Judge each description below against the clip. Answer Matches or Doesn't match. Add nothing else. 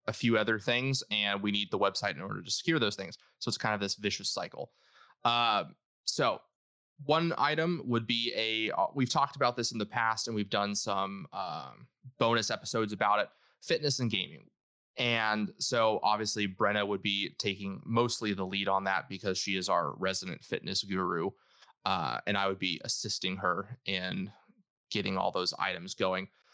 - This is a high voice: Doesn't match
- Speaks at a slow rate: Doesn't match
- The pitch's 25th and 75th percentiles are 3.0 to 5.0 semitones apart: Matches